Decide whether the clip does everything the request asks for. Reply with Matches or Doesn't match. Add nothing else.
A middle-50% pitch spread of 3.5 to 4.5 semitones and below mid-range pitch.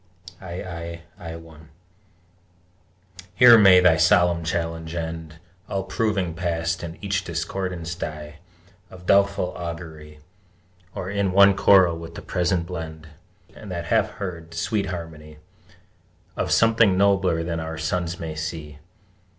Doesn't match